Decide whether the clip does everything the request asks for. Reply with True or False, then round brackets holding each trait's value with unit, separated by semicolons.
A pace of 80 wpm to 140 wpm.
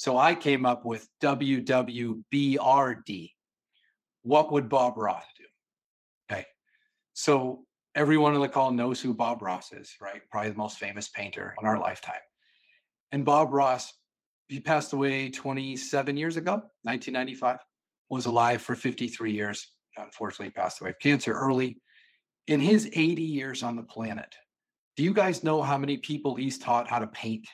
False (155 wpm)